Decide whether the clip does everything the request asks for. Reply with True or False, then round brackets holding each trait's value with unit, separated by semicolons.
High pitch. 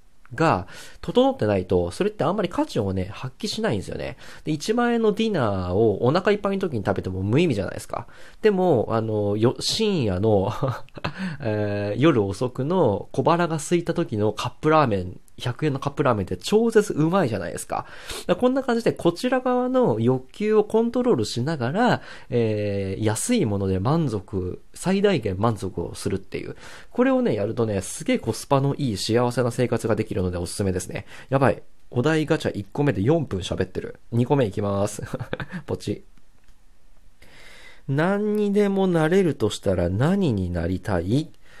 False (130 Hz)